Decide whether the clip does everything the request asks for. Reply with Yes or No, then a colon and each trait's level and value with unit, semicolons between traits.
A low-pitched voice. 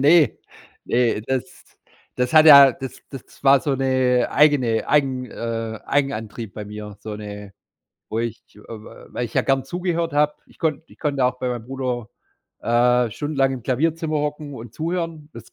Yes: low, 130 Hz